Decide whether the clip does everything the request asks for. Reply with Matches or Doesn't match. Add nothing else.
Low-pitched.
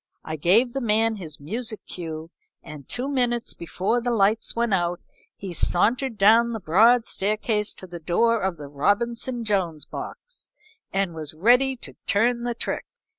Doesn't match